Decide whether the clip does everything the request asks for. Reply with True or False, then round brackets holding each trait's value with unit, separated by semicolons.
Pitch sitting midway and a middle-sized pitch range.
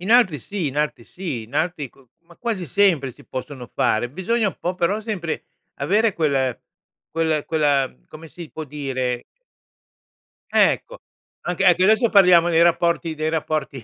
True (160 Hz; 4.8 semitones)